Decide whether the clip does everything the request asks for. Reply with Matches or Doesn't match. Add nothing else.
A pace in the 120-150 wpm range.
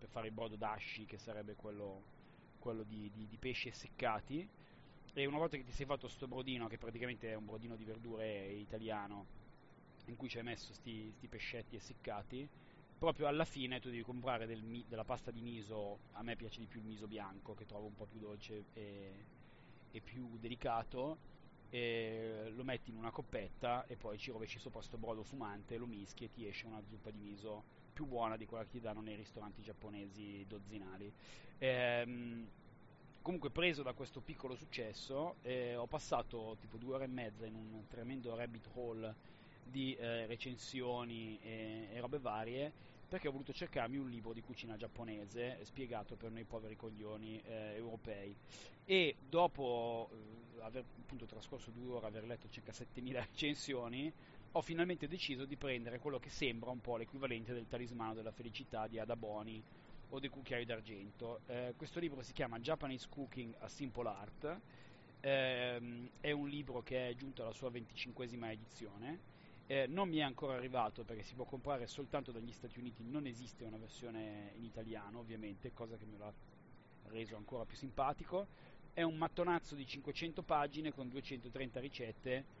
Doesn't match